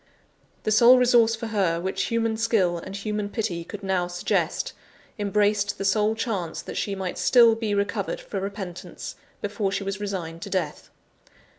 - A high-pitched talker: Yes, high, 205 Hz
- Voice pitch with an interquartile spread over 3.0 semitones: No, average, 2.7 semitones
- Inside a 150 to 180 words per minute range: Yes, average, 165 wpm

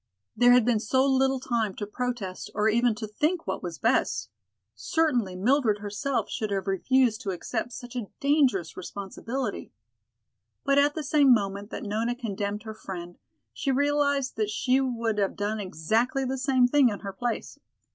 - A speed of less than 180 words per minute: Yes, average, 170 wpm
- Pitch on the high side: Yes, high, 230 Hz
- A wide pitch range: No, average, 4.6 semitones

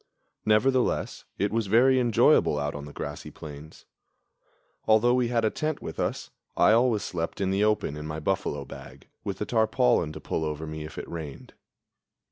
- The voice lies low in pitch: Yes, low, 100 Hz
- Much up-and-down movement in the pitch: Yes, wide, 6.9 semitones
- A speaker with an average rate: Yes, average, 185 wpm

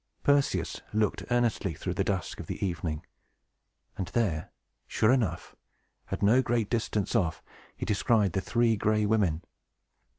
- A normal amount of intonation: Yes, average, 3.8 semitones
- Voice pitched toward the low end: Yes, low, 105 Hz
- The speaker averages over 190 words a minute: No, average, 140 wpm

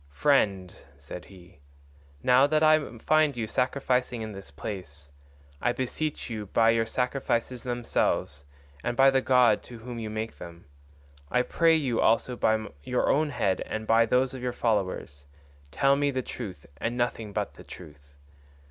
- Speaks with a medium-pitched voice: No, low, 115 Hz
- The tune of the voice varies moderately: Yes, average, 4.5 semitones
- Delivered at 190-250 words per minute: No, average, 165 wpm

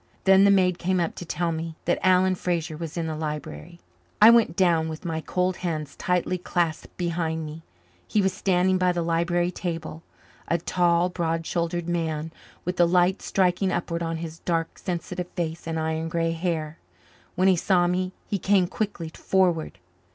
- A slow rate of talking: No, average, 180 wpm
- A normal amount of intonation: No, narrow, 1.9 semitones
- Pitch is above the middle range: No, medium, 175 Hz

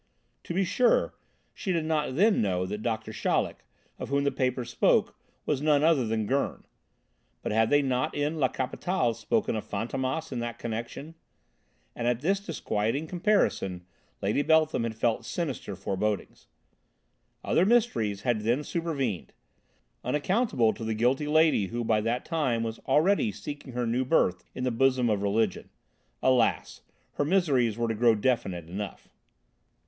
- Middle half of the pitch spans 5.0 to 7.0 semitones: Yes, wide, 5.5 semitones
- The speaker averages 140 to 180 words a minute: Yes, average, 155 wpm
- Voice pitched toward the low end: Yes, low, 125 Hz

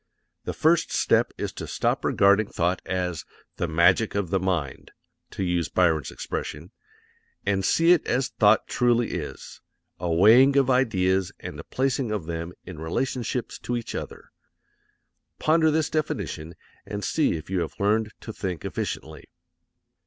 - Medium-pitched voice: No, very low, 95 Hz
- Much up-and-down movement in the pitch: Yes, wide, 6.1 semitones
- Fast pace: No, average, 150 wpm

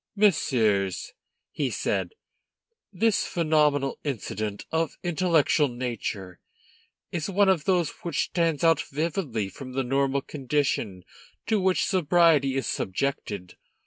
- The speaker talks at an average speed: No, slow, 115 wpm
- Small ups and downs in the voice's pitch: No, wide, 5.6 semitones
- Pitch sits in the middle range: Yes, medium, 145 Hz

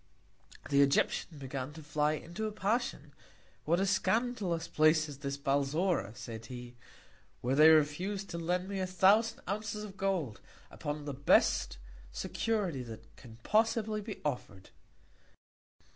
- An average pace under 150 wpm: Yes, average, 140 wpm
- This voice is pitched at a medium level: Yes, medium, 160 Hz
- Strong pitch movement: Yes, wide, 6.2 semitones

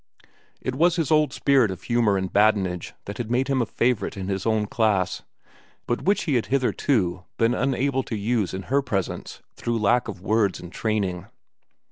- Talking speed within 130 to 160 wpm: No, average, 185 wpm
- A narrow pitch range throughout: No, average, 4.7 semitones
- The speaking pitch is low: Yes, low, 115 Hz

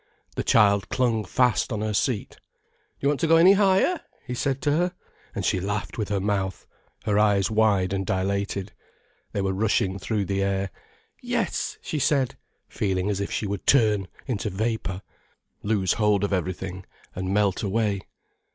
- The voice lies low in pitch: Yes, low, 105 Hz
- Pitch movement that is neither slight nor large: Yes, average, 3.0 semitones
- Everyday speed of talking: Yes, average, 170 wpm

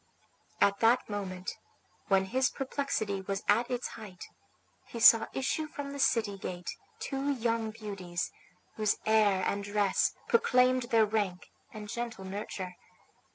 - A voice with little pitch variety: No, average, 3.8 semitones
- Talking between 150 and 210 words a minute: No, slow, 135 wpm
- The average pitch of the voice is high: Yes, high, 215 Hz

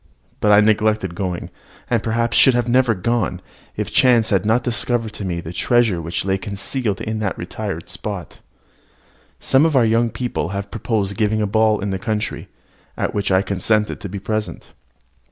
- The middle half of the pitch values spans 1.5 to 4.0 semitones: Yes, average, 2.9 semitones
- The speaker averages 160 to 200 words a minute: Yes, average, 180 wpm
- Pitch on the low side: Yes, low, 105 Hz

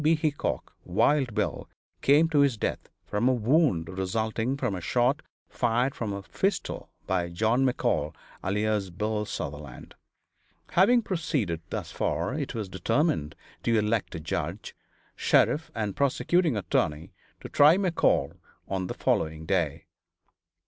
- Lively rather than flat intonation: Yes, wide, 7.3 semitones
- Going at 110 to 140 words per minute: Yes, slow, 135 wpm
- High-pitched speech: No, low, 110 Hz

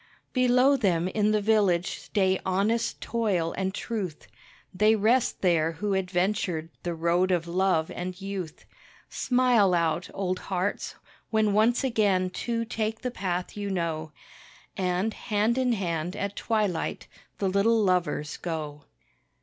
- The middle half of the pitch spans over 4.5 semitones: No, average, 3.6 semitones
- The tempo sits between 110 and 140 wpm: Yes, slow, 135 wpm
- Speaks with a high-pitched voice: Yes, high, 195 Hz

